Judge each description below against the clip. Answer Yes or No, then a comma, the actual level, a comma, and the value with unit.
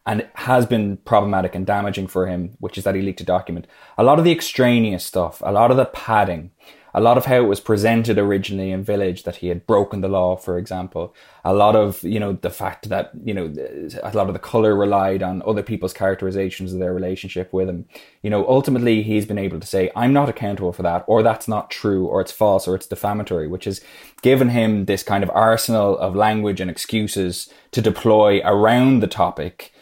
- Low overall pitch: Yes, low, 100 Hz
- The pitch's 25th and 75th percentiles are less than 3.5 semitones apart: Yes, average, 2.8 semitones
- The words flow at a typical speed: No, fast, 220 wpm